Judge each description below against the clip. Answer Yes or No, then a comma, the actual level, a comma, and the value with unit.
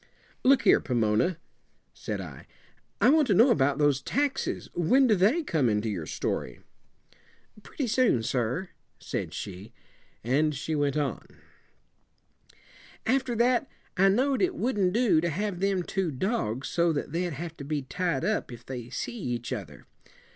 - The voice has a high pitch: No, medium, 170 Hz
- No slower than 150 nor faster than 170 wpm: Yes, average, 155 wpm